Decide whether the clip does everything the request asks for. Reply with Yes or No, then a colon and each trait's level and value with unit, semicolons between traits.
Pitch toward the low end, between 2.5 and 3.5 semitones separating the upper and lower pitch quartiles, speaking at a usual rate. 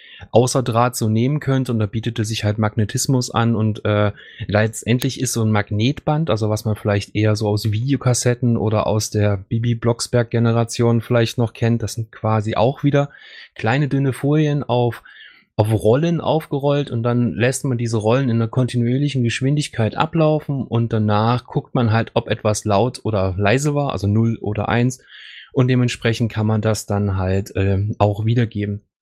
Yes: low, 115 Hz; average, 2.9 semitones; average, 170 wpm